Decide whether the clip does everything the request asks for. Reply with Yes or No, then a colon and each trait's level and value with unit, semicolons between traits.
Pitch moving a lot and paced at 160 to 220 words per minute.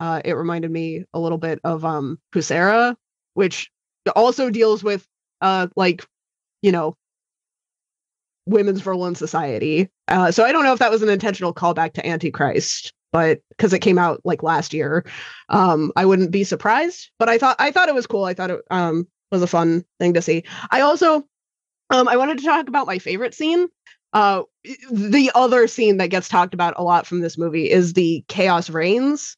Yes: wide, 5.9 semitones; average, 190 wpm